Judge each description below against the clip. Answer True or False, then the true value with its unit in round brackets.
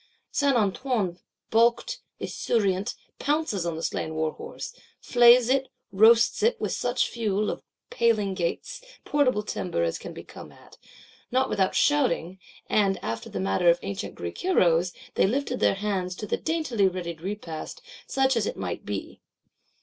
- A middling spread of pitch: False (5.8 semitones)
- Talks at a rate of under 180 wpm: True (150 wpm)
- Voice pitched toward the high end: True (205 Hz)